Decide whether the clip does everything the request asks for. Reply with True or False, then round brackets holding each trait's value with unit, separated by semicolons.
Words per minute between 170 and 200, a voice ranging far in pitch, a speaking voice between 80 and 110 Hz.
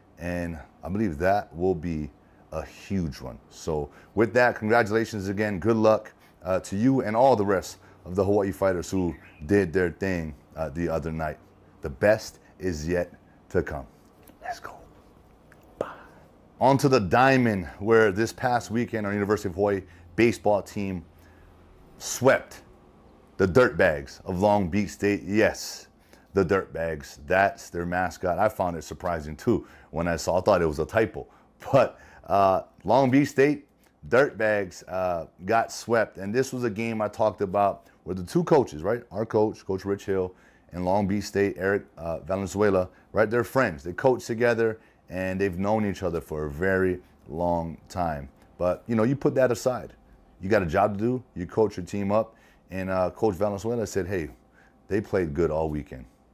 False (180 wpm; 4.0 semitones; 95 Hz)